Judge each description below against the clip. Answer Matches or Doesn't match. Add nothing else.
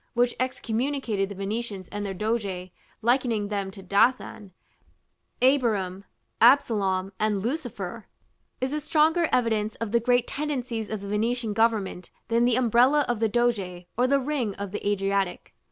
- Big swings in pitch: Doesn't match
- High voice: Matches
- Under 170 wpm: Matches